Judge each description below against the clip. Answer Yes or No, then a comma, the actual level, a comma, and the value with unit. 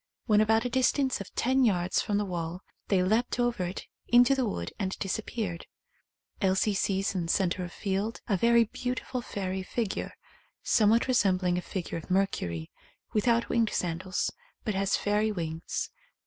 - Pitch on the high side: Yes, high, 200 Hz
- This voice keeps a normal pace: Yes, average, 160 wpm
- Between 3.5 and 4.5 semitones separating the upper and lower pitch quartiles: Yes, average, 4.0 semitones